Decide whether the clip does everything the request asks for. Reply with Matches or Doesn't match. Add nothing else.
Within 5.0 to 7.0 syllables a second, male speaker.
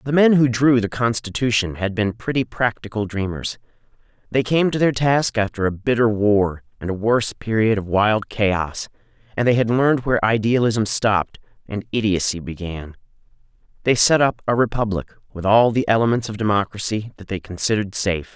Matches